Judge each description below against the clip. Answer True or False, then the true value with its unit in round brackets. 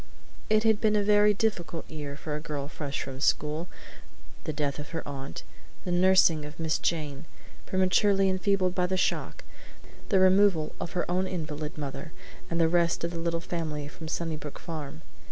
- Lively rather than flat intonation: False (3.8 semitones)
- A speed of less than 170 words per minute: False (175 wpm)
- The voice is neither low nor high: True (165 Hz)